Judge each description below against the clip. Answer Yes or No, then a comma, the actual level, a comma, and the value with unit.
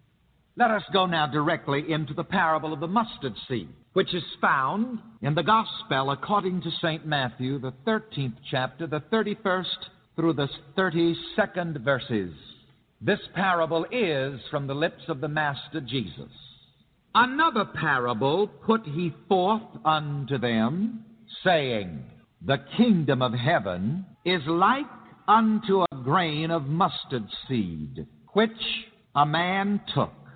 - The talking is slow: Yes, slow, 130 wpm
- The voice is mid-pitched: Yes, medium, 170 Hz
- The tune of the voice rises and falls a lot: Yes, wide, 6.0 semitones